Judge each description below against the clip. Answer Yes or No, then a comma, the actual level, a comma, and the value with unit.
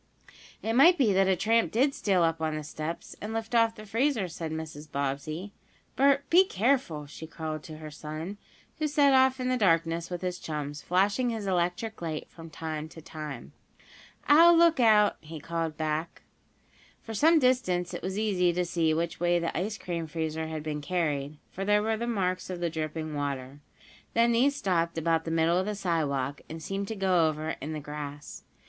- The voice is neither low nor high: Yes, medium, 175 Hz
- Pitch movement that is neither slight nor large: No, wide, 5.7 semitones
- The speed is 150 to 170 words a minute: No, average, 195 wpm